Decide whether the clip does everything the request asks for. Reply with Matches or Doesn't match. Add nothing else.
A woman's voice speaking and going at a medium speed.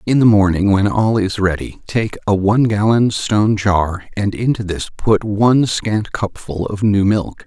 Doesn't match